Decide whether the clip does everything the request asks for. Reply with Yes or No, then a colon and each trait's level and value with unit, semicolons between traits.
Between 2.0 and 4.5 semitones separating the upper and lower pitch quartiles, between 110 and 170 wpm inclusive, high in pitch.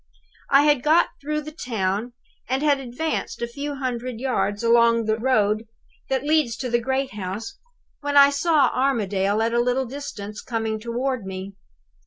Yes: average, 4.0 semitones; average, 165 wpm; high, 245 Hz